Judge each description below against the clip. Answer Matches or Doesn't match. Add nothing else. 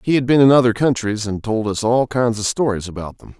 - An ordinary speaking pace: Doesn't match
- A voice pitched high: Doesn't match